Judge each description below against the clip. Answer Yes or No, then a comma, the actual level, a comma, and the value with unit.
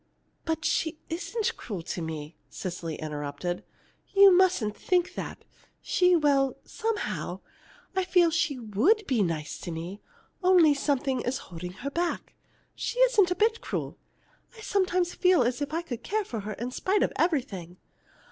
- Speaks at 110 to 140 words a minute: No, average, 155 wpm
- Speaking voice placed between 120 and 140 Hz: No, very high, 290 Hz